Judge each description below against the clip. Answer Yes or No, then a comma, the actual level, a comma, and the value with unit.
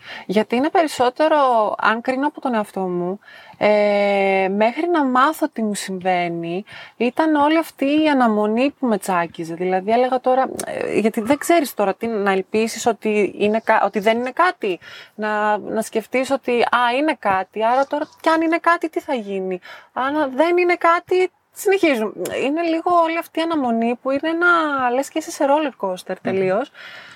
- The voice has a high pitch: Yes, very high, 250 Hz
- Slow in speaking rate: No, fast, 170 wpm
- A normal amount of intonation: No, wide, 6.8 semitones